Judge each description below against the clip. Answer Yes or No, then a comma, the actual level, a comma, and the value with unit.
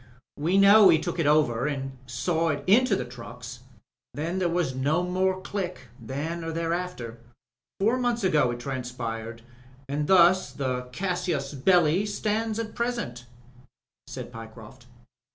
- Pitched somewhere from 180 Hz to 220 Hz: No, medium, 160 Hz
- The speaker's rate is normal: Yes, average, 145 wpm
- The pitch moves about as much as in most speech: No, wide, 6.9 semitones